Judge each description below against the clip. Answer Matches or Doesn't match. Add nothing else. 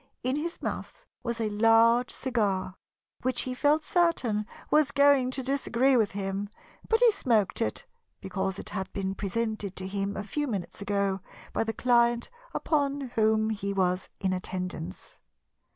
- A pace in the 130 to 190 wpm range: Matches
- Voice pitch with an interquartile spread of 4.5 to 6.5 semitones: Matches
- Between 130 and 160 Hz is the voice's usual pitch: Doesn't match